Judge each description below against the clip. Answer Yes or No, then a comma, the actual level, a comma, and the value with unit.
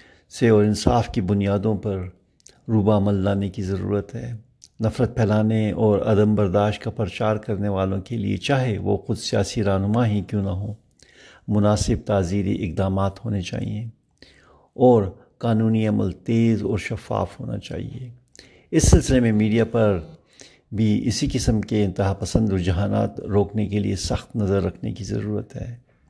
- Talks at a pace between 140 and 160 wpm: Yes, average, 150 wpm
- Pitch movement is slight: Yes, narrow, 2.3 semitones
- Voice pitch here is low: Yes, low, 105 Hz